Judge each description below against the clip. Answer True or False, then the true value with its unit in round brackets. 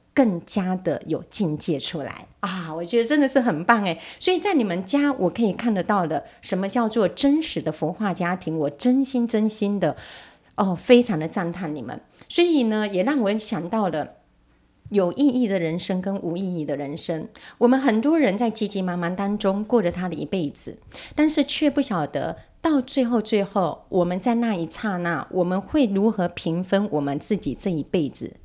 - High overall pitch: True (200 Hz)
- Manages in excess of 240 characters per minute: True (275 characters per minute)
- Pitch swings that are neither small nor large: False (5.9 semitones)